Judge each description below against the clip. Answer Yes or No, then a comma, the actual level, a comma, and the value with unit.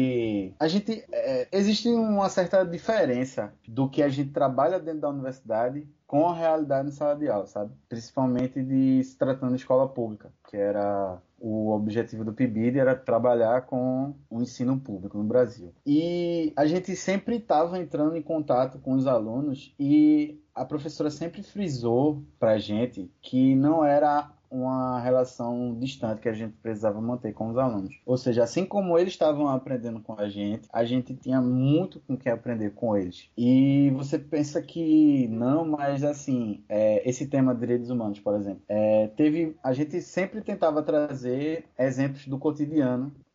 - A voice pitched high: No, low, 130 Hz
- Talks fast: No, average, 165 wpm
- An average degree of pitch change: Yes, average, 4.5 semitones